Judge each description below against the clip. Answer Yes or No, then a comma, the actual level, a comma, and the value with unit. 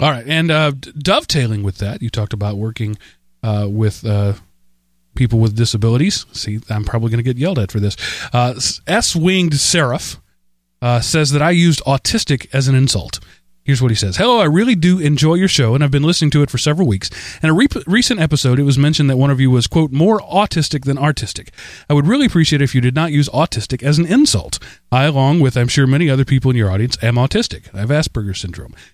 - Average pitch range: No, wide, 6.0 semitones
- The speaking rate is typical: No, fast, 220 wpm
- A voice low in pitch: Yes, low, 130 Hz